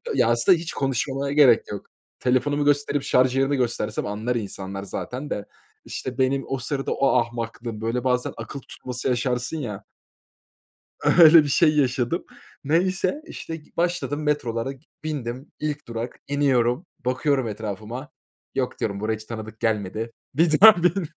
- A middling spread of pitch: Yes, average, 4.0 semitones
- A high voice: No, low, 130 Hz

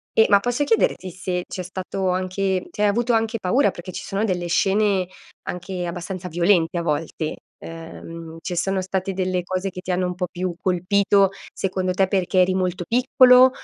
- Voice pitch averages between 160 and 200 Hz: Yes, medium, 185 Hz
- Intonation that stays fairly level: Yes, narrow, 1.8 semitones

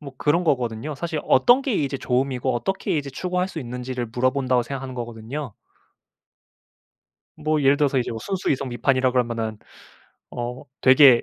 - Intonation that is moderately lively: Yes, average, 3.3 semitones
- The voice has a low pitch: Yes, low, 130 Hz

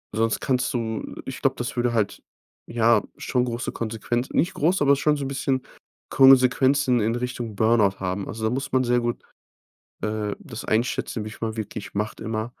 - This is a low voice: Yes, low, 120 Hz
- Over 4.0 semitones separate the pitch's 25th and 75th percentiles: No, average, 2.9 semitones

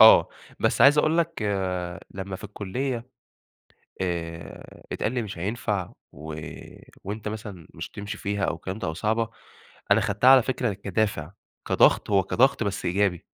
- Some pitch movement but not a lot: Yes, average, 3.6 semitones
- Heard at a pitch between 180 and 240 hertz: No, low, 105 Hz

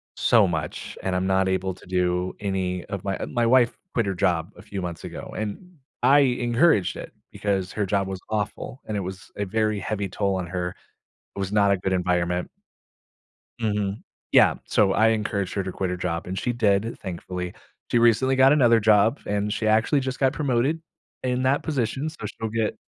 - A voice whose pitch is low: Yes, low, 105 Hz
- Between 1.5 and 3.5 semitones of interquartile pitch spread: No, average, 4.0 semitones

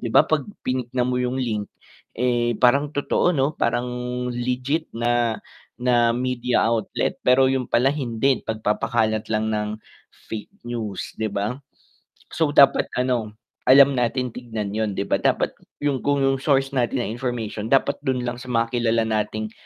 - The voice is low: Yes, low, 120 Hz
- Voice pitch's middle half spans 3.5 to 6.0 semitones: No, average, 2.7 semitones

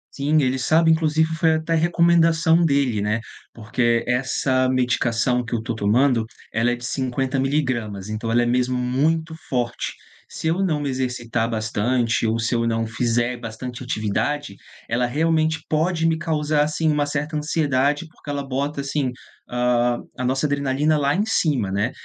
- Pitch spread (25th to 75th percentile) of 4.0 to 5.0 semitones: Yes, average, 4.3 semitones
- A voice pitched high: No, low, 130 Hz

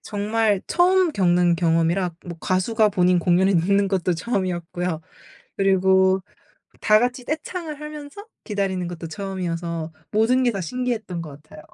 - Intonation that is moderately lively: Yes, average, 4.5 semitones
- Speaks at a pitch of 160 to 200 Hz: Yes, high, 190 Hz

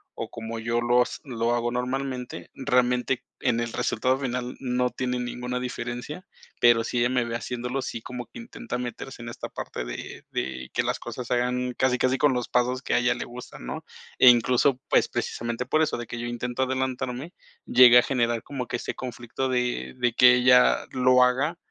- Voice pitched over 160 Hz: No, low, 125 Hz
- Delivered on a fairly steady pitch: Yes, narrow, 1.2 semitones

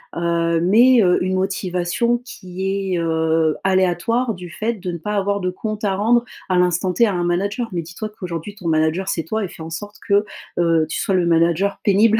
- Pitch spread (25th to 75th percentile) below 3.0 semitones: No, average, 3.3 semitones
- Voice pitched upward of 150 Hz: Yes, medium, 185 Hz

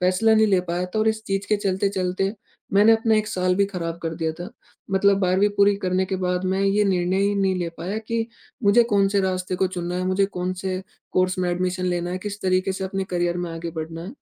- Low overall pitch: No, medium, 185 Hz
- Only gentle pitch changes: Yes, narrow, 1.9 semitones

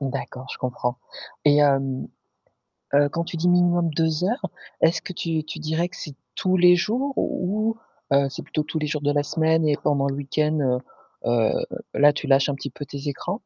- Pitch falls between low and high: Yes, medium, 150 Hz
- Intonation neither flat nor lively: Yes, average, 3.7 semitones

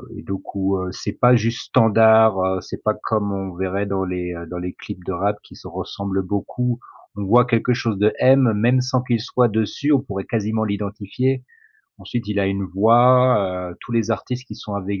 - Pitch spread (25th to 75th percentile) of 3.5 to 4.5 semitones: Yes, average, 3.8 semitones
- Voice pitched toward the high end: No, low, 105 Hz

